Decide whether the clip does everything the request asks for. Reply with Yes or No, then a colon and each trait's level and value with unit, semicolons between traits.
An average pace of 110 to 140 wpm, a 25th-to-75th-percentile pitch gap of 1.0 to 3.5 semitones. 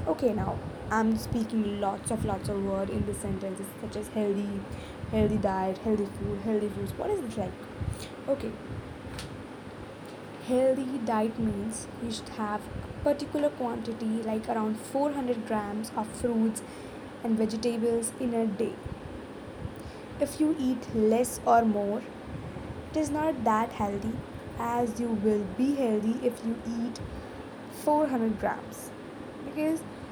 Yes: slow, 135 wpm; average, 3.1 semitones